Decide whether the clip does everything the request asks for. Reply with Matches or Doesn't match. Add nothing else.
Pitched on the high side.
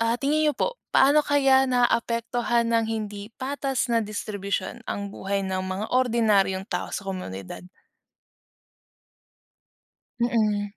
Matches